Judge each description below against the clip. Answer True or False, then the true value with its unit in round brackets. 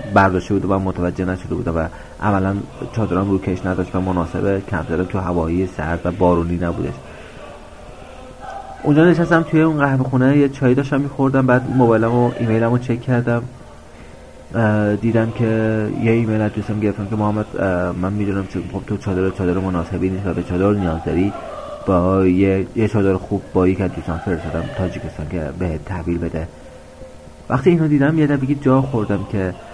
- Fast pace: True (165 wpm)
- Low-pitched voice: True (95 Hz)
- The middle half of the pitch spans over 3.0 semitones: True (4.5 semitones)